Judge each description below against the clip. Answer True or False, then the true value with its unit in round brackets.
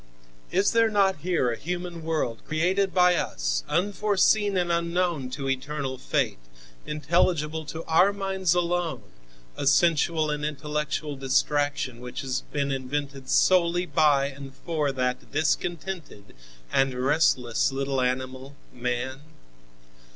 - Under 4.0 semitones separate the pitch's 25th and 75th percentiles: False (4.7 semitones)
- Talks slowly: True (120 wpm)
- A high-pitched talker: False (150 Hz)